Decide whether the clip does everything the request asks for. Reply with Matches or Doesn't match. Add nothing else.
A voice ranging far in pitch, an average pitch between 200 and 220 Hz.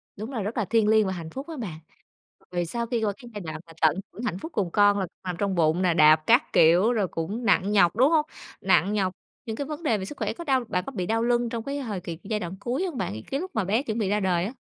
Doesn't match